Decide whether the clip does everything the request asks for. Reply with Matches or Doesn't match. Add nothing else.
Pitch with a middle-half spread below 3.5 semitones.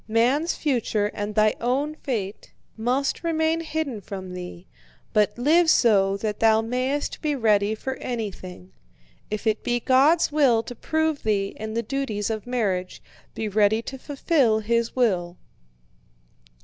Doesn't match